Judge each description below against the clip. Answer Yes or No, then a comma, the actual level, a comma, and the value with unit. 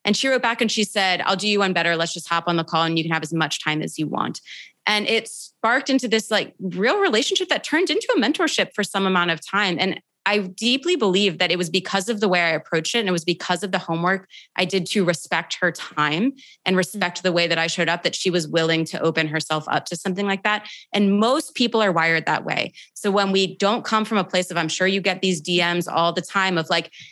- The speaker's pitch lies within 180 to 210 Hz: Yes, high, 190 Hz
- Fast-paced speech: Yes, fast, 265 wpm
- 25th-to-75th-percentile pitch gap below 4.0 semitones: Yes, average, 3.6 semitones